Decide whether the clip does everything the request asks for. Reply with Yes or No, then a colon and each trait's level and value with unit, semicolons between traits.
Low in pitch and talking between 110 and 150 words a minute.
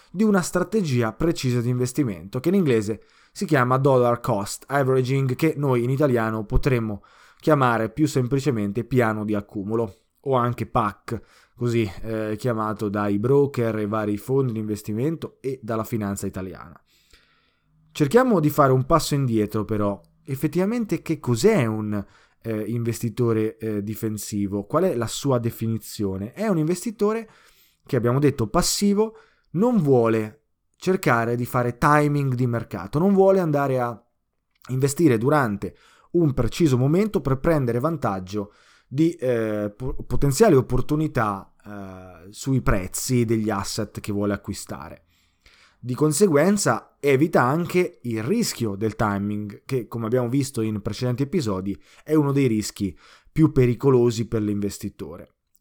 Yes: low, 120 Hz; average, 135 wpm